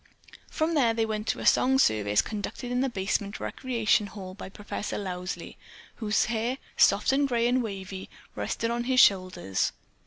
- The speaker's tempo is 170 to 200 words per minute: No, average, 160 wpm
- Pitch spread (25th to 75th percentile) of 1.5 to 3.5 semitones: No, average, 3.9 semitones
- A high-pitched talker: Yes, high, 215 Hz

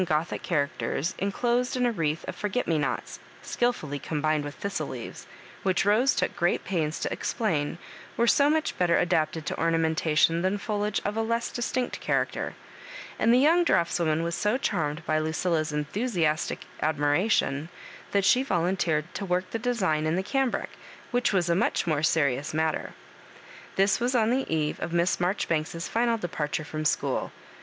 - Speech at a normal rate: Yes, average, 170 wpm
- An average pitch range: No, wide, 6.1 semitones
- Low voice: No, medium, 175 Hz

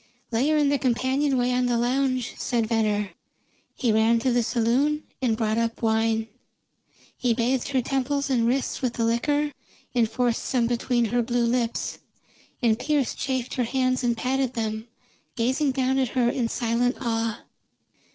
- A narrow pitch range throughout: Yes, narrow, 2.3 semitones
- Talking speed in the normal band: Yes, average, 165 wpm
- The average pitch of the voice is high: Yes, high, 245 Hz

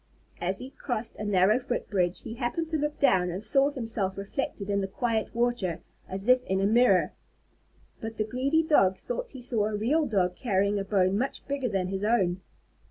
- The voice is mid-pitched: No, high, 215 Hz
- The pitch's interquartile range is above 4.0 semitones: Yes, average, 4.6 semitones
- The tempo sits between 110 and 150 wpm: No, average, 195 wpm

